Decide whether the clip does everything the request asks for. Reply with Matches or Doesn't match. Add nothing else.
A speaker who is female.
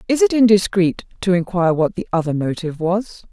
Matches